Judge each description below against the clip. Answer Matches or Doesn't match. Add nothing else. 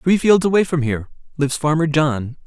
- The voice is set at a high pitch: Doesn't match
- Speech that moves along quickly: Doesn't match